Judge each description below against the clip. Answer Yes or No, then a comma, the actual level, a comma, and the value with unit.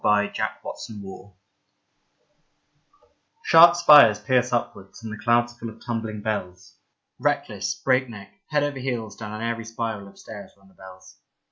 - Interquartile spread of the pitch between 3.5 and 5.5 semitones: No, average, 2.9 semitones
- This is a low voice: Yes, low, 110 Hz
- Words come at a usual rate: Yes, average, 150 wpm